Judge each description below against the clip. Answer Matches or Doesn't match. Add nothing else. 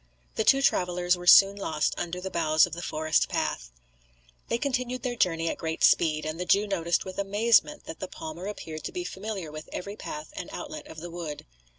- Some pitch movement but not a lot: Matches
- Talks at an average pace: Doesn't match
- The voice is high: Doesn't match